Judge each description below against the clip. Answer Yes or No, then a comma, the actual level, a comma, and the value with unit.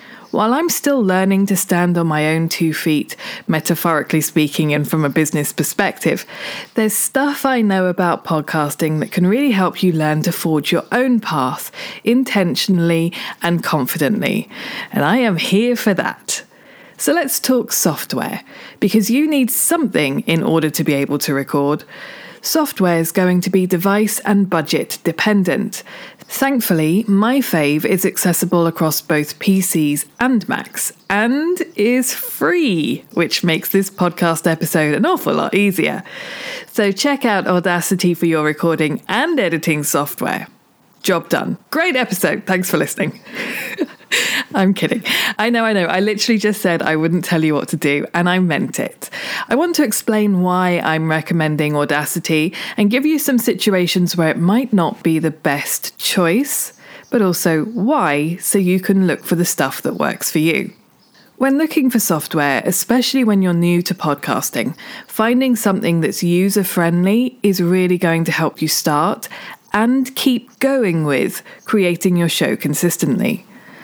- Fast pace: No, average, 155 wpm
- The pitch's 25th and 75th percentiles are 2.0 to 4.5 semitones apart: No, wide, 5.4 semitones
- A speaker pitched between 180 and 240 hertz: Yes, medium, 185 Hz